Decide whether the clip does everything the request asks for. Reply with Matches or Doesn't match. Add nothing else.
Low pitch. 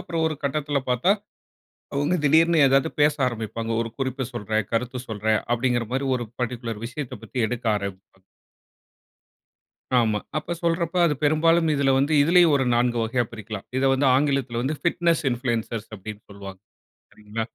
Matches